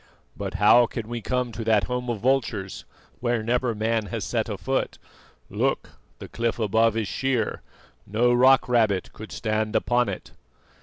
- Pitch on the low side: Yes, low, 115 Hz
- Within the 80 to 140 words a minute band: No, average, 165 wpm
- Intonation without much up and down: Yes, narrow, 2.1 semitones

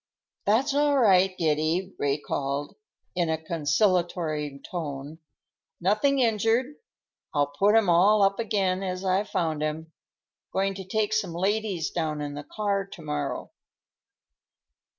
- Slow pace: Yes, slow, 130 wpm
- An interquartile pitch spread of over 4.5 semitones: Yes, average, 5.0 semitones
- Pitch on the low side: No, medium, 185 Hz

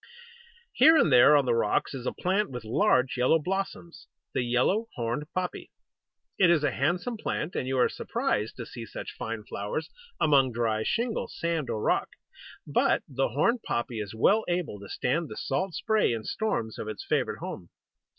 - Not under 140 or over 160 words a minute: No, average, 180 wpm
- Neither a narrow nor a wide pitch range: No, wide, 7.2 semitones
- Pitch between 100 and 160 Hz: Yes, low, 135 Hz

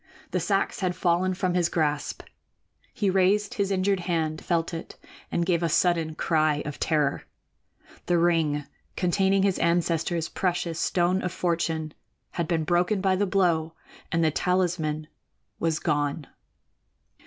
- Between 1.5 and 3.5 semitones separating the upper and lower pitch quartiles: Yes, narrow, 2.5 semitones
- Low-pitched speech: No, medium, 170 Hz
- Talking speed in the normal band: Yes, average, 145 wpm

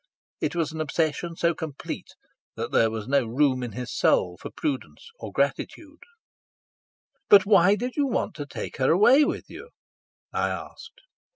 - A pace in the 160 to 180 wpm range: Yes, average, 165 wpm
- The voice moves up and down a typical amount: No, wide, 8.8 semitones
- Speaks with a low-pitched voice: No, medium, 160 Hz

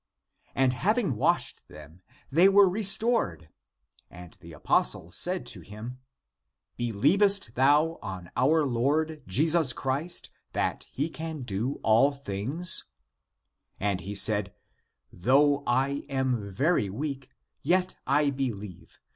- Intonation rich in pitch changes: Yes, wide, 7.3 semitones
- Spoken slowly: Yes, slow, 125 wpm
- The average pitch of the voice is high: No, low, 135 Hz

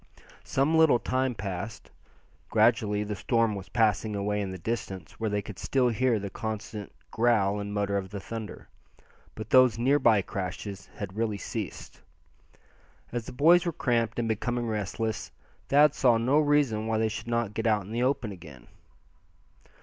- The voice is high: No, low, 110 Hz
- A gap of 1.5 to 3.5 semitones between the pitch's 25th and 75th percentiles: Yes, average, 2.9 semitones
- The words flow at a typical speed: Yes, average, 170 wpm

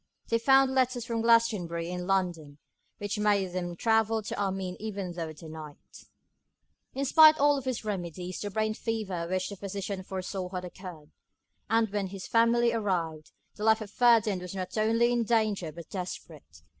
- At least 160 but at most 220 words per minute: Yes, average, 170 wpm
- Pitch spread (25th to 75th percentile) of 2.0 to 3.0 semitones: No, average, 4.0 semitones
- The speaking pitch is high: Yes, high, 200 Hz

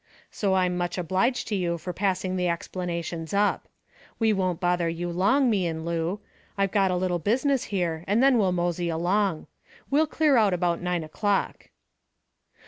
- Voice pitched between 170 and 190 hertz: Yes, medium, 185 Hz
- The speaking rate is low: No, average, 170 wpm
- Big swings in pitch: No, average, 2.9 semitones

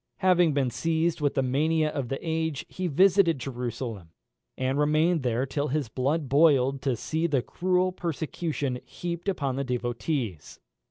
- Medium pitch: Yes, medium, 145 Hz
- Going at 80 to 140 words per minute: No, average, 155 wpm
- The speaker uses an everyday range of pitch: Yes, average, 4.2 semitones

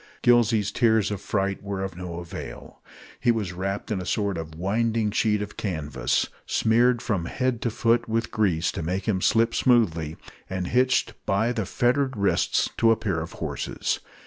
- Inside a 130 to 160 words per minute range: No, average, 175 wpm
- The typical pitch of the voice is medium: No, low, 105 Hz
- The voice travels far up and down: No, average, 3.9 semitones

